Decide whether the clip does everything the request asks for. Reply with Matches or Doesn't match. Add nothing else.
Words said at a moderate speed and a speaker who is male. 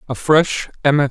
Matches